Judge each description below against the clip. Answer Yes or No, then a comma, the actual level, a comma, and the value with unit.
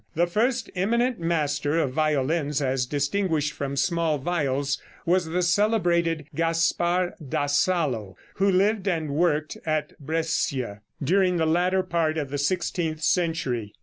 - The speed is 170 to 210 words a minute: No, slow, 135 wpm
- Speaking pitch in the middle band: Yes, medium, 165 Hz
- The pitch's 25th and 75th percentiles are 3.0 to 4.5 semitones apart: Yes, average, 3.6 semitones